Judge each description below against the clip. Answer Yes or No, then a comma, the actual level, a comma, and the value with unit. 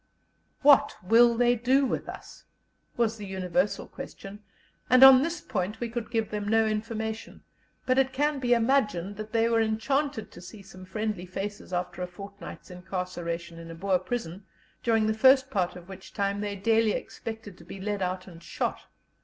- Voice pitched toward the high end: Yes, high, 210 Hz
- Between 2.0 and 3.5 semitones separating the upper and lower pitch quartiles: No, average, 4.0 semitones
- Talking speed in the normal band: Yes, average, 180 wpm